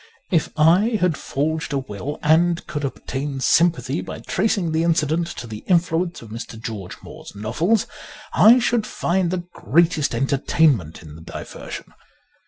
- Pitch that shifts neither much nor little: Yes, average, 4.8 semitones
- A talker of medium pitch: Yes, medium, 160 Hz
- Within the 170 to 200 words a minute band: No, average, 150 wpm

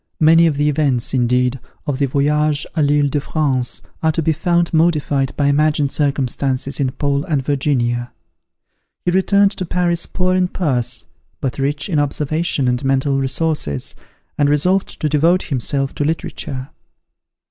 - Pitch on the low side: No, medium, 145 Hz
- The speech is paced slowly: No, average, 155 wpm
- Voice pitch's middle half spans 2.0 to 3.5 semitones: Yes, average, 2.8 semitones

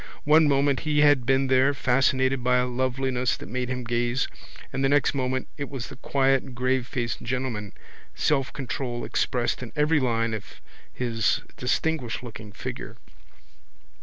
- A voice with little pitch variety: Yes, narrow, 1.9 semitones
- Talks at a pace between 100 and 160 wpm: Yes, average, 140 wpm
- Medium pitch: No, low, 130 Hz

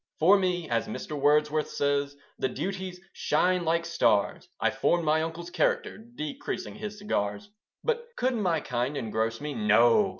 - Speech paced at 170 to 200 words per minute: No, average, 155 wpm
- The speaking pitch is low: No, medium, 160 Hz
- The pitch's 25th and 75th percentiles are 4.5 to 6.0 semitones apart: Yes, average, 5.0 semitones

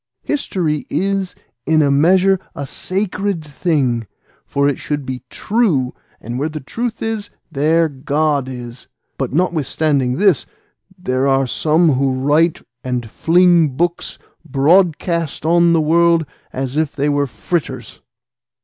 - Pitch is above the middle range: No, medium, 155 Hz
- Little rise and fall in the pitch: No, average, 4.3 semitones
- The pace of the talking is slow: Yes, slow, 130 wpm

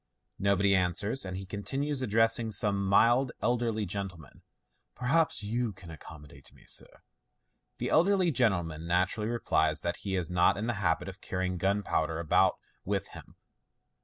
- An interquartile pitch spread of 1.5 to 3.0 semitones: No, average, 4.7 semitones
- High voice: No, low, 100 Hz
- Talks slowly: No, average, 160 wpm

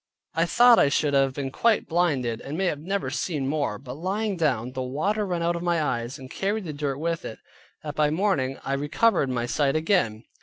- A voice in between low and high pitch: Yes, medium, 150 Hz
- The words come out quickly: Yes, fast, 220 wpm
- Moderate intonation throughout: Yes, average, 4.8 semitones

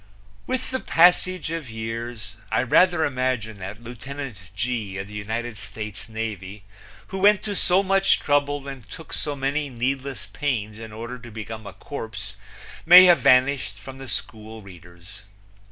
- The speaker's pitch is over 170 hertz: No, low, 120 Hz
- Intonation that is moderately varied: Yes, average, 5.0 semitones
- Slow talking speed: No, average, 155 wpm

